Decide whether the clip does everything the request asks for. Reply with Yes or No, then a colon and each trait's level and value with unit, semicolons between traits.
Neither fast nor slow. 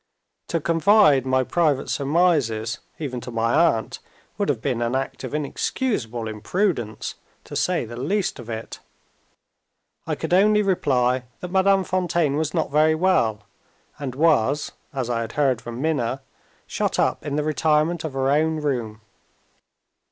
Yes: average, 150 wpm